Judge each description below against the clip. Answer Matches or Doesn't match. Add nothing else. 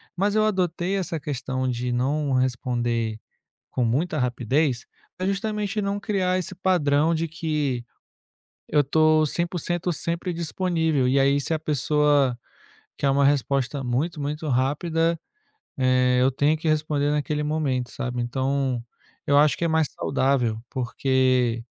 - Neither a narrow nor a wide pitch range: Matches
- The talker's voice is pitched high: Doesn't match